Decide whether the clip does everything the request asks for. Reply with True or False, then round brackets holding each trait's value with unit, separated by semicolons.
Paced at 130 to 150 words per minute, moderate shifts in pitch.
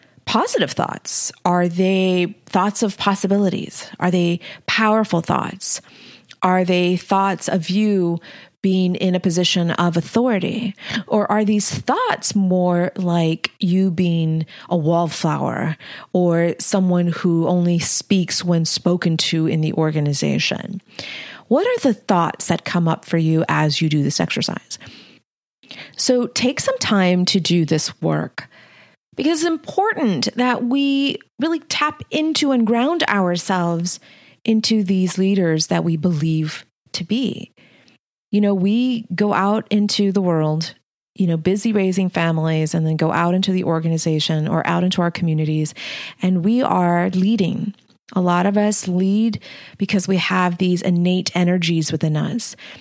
True (145 wpm; 3.4 semitones)